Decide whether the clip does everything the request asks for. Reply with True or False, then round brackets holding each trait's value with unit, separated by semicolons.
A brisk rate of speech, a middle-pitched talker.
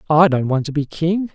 True (270 wpm; 160 Hz)